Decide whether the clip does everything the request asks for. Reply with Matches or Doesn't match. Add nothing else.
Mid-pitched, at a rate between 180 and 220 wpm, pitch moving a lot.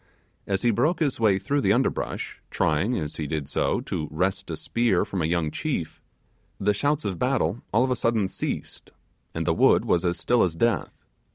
Doesn't match